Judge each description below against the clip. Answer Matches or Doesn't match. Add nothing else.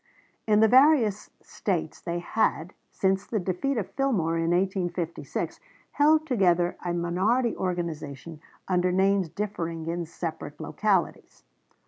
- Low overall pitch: Doesn't match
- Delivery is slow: Matches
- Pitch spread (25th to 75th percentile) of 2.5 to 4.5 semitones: Matches